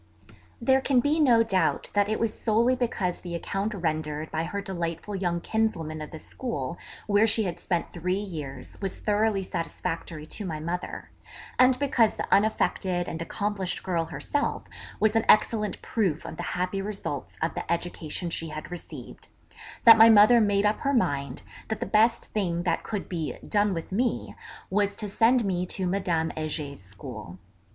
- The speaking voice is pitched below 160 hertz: No, high, 195 Hz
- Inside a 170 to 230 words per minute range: Yes, average, 175 wpm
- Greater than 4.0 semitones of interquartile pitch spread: Yes, average, 4.7 semitones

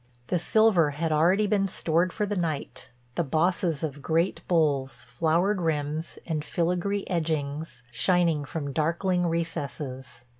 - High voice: No, medium, 165 Hz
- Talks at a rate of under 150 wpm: Yes, slow, 135 wpm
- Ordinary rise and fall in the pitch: Yes, average, 3.1 semitones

